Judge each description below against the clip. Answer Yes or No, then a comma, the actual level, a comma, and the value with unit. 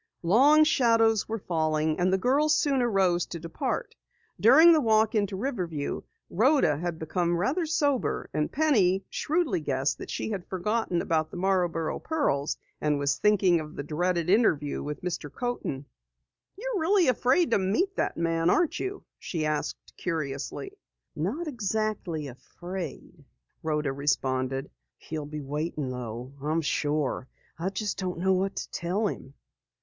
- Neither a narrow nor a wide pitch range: No, wide, 6.9 semitones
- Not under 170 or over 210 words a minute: No, average, 145 wpm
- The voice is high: No, medium, 180 Hz